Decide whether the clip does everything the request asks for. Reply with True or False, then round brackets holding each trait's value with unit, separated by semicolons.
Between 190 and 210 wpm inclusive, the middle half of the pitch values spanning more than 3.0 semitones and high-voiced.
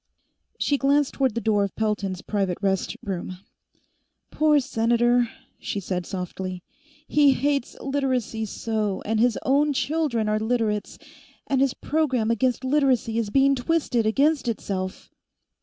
False (135 wpm; 4.7 semitones; 235 Hz)